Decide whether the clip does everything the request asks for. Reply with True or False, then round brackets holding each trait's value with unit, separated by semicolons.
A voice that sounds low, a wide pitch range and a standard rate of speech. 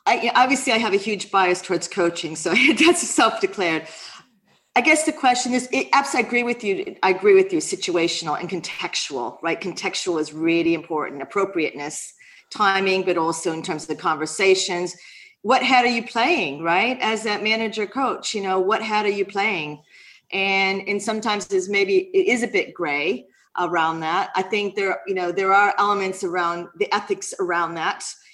False (200 Hz; 6.1 semitones; 180 wpm)